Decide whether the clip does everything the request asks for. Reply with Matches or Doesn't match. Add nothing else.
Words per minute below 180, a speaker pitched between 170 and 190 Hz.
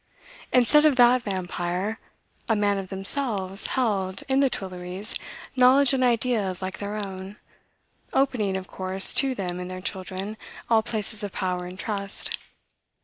Doesn't match